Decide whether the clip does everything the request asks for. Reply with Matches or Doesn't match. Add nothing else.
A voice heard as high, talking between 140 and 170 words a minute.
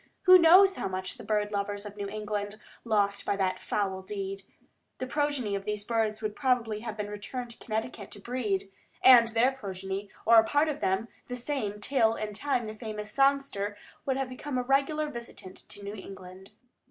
Doesn't match